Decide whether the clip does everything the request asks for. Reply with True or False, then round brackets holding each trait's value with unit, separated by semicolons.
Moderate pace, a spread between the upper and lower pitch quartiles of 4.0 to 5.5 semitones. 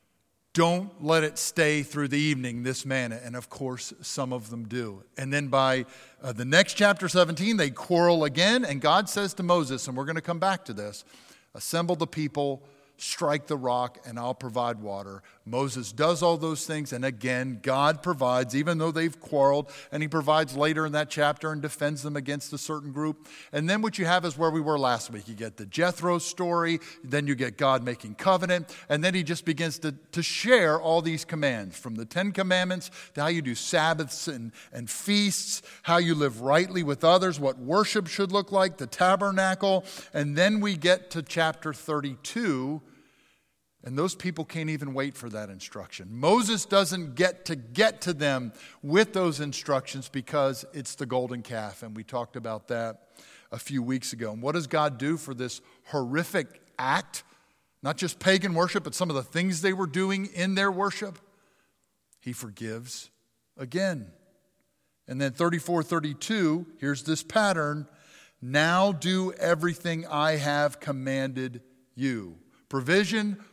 True (175 wpm; 5.2 semitones)